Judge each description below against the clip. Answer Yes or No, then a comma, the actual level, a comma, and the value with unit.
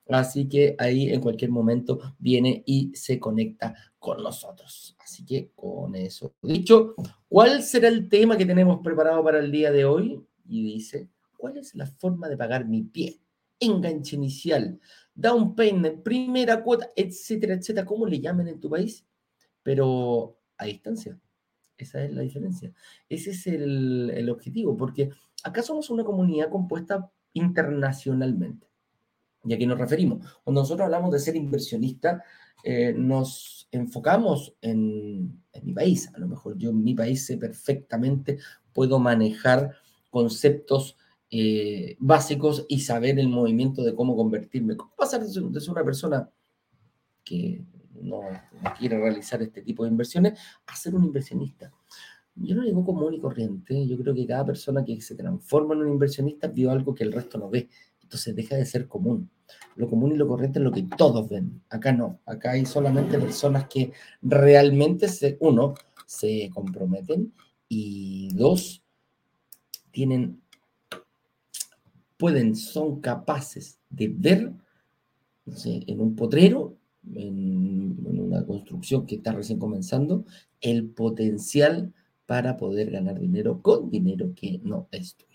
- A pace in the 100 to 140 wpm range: No, average, 150 wpm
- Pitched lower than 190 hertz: Yes, medium, 140 Hz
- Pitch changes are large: Yes, wide, 7.0 semitones